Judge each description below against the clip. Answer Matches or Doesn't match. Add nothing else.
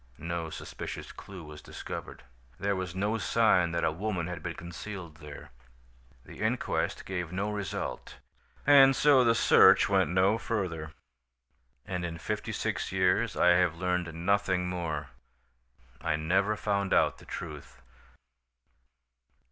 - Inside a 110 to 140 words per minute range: Matches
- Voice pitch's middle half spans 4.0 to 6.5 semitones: Doesn't match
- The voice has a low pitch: Matches